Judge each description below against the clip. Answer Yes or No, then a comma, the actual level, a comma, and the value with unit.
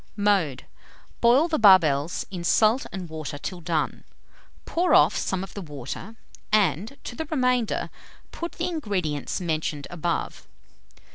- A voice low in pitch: No, high, 190 Hz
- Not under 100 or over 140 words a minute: Yes, slow, 135 wpm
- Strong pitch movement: Yes, wide, 7.0 semitones